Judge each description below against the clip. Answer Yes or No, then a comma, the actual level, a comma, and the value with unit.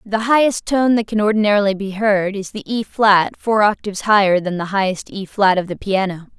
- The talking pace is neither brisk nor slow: Yes, average, 195 wpm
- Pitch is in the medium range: No, high, 205 Hz